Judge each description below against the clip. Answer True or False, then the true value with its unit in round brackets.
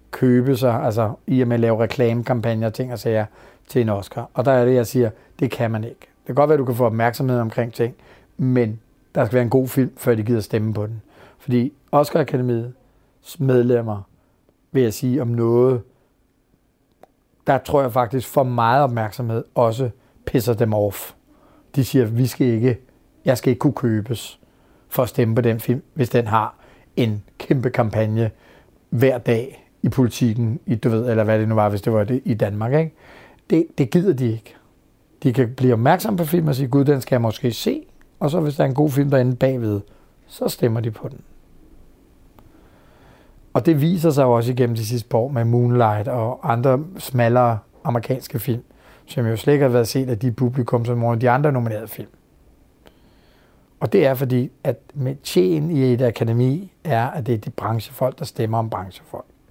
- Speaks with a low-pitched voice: True (125 Hz)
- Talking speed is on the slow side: False (195 wpm)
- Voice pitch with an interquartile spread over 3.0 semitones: False (2.6 semitones)